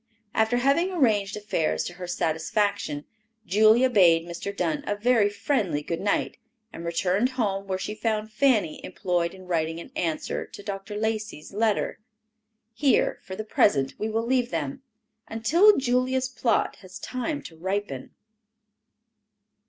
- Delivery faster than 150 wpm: No, average, 145 wpm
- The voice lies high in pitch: Yes, high, 205 Hz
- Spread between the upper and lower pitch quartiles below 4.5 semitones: No, average, 4.9 semitones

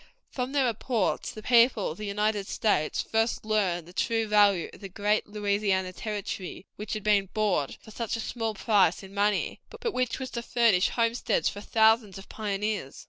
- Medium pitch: No, high, 210 Hz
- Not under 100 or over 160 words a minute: No, average, 185 wpm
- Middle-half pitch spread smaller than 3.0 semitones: Yes, narrow, 2.4 semitones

